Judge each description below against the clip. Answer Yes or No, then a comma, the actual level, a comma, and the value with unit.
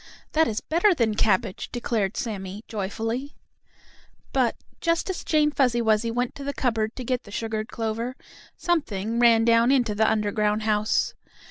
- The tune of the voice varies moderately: Yes, average, 3.0 semitones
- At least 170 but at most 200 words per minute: No, average, 155 wpm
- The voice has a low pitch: No, high, 230 Hz